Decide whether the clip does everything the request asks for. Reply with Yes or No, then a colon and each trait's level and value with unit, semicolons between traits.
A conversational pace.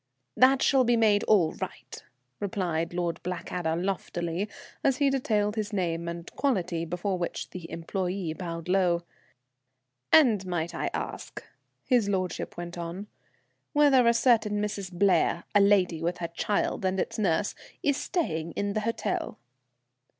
Yes: average, 145 wpm